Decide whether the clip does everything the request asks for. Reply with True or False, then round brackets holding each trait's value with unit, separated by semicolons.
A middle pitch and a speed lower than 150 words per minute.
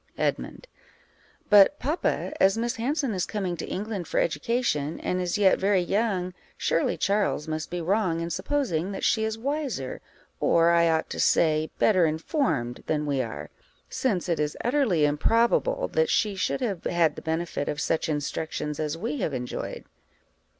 False (180 Hz; 165 wpm)